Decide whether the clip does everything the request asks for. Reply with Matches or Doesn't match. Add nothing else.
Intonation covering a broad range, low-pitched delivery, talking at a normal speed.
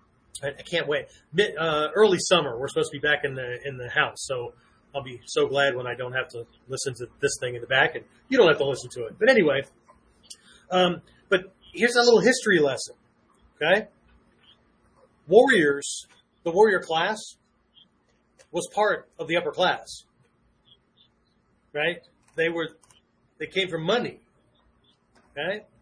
Doesn't match